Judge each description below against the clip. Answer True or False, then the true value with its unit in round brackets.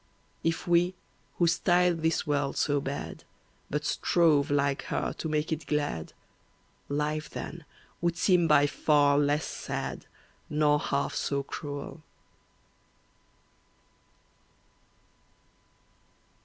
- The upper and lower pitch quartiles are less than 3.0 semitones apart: True (2.4 semitones)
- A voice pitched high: False (150 Hz)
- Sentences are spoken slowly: True (100 wpm)